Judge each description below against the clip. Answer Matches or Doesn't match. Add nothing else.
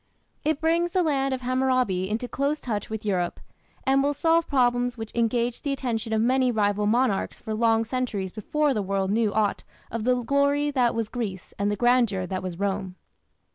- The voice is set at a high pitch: Matches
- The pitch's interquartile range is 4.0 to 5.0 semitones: Matches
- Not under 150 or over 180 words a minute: Doesn't match